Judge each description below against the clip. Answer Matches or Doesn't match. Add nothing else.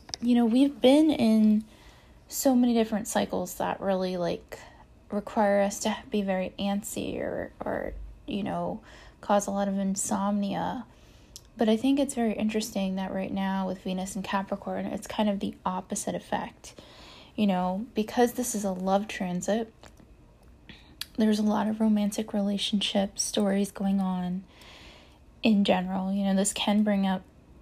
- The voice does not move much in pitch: Matches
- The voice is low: Doesn't match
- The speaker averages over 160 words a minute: Doesn't match